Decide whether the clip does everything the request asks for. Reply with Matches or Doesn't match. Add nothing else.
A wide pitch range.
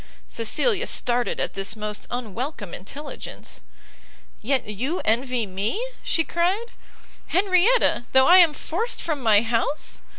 Matches